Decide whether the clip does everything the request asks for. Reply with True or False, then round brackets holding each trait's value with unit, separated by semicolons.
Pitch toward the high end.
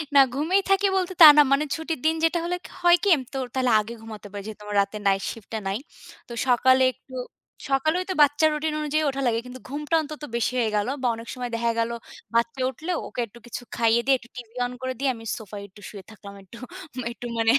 True (250 Hz)